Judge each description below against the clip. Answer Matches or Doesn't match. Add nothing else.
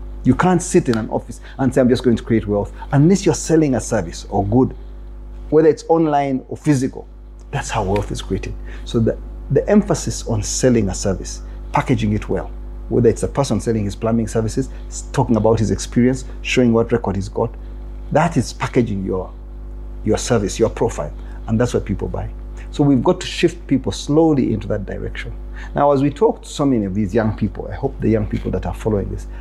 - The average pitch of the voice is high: Doesn't match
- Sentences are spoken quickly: Matches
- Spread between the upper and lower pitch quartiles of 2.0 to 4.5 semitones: Doesn't match